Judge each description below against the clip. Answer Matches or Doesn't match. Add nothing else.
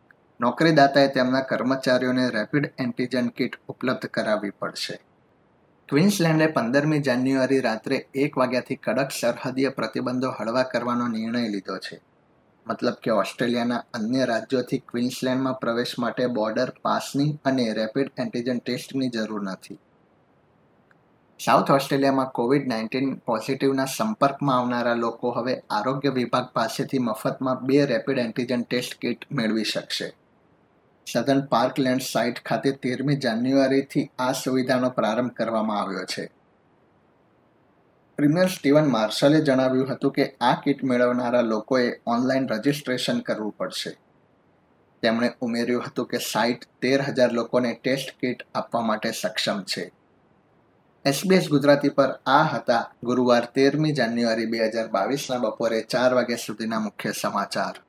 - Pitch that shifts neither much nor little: Doesn't match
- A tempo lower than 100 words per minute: Doesn't match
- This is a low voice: Matches